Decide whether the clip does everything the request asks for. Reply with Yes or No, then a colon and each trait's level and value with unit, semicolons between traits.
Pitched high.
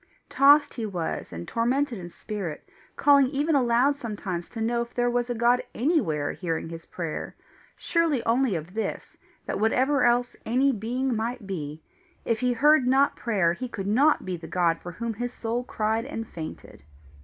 Yes: high, 235 Hz